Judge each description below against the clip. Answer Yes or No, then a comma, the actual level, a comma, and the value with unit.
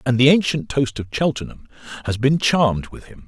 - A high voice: No, low, 130 Hz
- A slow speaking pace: No, average, 200 wpm